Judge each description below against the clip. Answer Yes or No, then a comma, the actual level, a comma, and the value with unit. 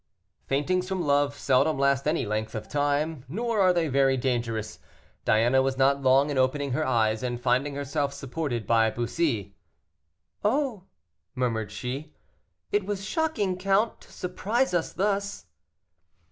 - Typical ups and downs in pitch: No, wide, 6.3 semitones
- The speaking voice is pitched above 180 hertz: No, medium, 140 Hz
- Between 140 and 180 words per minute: Yes, average, 145 wpm